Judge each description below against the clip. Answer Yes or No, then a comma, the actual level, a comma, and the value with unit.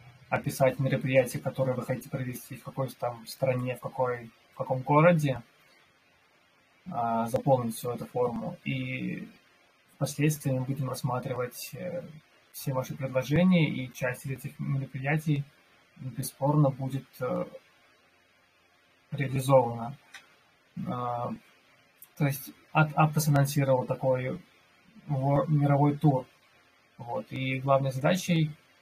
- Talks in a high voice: No, low, 135 Hz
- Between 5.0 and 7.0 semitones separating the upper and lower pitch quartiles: No, average, 2.8 semitones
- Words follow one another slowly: Yes, slow, 100 wpm